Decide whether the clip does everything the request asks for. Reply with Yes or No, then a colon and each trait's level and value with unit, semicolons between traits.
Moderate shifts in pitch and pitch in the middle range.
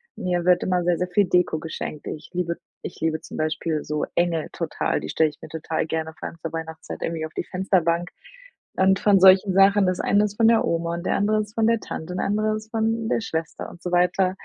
Yes: average, 3.4 semitones; medium, 180 Hz